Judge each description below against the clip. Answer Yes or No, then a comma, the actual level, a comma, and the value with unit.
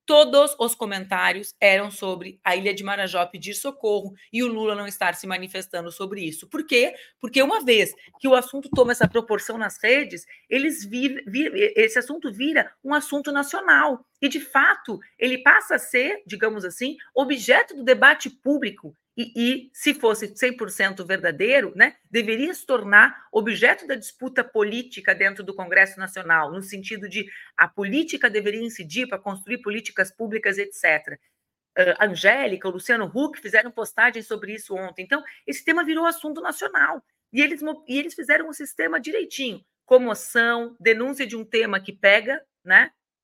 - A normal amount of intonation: No, wide, 5.9 semitones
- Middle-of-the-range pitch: No, high, 235 Hz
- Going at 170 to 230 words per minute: No, average, 160 wpm